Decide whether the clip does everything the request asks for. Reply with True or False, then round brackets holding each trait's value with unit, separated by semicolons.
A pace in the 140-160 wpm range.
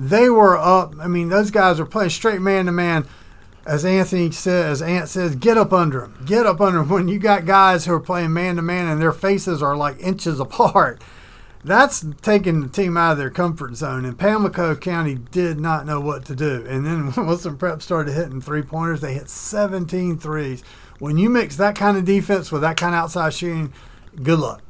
False (205 wpm)